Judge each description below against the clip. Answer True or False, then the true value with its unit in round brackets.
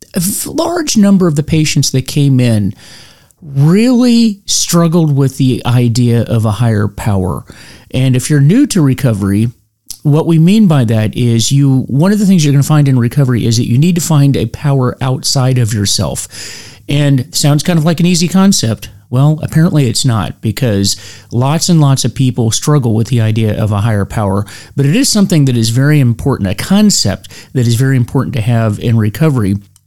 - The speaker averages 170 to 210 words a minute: True (195 wpm)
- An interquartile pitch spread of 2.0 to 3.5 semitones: False (5.5 semitones)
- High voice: False (130 Hz)